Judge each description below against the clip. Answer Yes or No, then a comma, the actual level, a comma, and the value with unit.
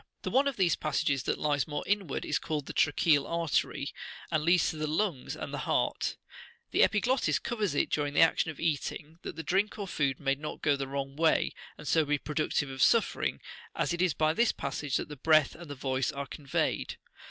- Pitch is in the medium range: Yes, medium, 155 Hz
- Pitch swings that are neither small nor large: Yes, average, 3.3 semitones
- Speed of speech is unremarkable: No, fast, 215 wpm